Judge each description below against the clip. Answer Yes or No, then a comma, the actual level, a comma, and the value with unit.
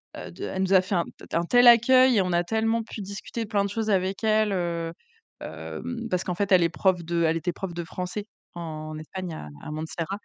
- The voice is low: No, medium, 185 Hz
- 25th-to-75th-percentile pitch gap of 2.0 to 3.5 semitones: No, average, 4.0 semitones